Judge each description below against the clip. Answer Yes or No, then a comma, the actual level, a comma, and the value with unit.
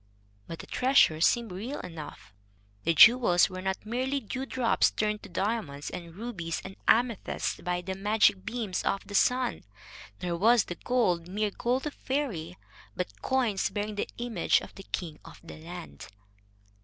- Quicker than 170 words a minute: No, average, 160 wpm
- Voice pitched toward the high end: Yes, high, 205 Hz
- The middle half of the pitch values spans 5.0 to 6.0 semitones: Yes, average, 5.3 semitones